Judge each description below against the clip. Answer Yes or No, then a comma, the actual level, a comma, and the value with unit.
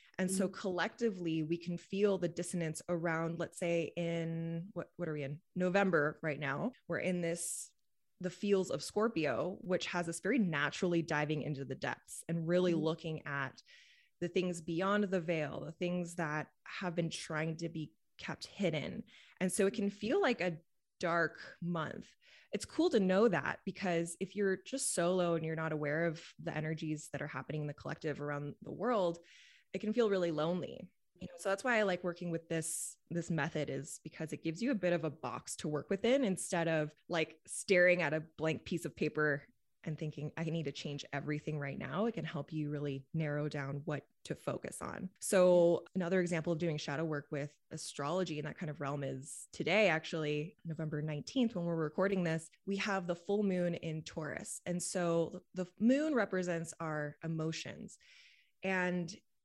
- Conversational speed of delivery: Yes, average, 190 wpm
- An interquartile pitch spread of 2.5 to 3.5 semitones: Yes, average, 3.0 semitones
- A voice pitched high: No, medium, 170 Hz